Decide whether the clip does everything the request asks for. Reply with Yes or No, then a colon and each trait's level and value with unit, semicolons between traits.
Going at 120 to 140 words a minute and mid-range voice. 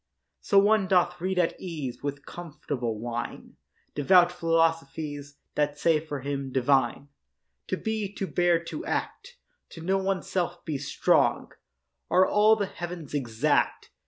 Yes: slow, 135 wpm; medium, 165 Hz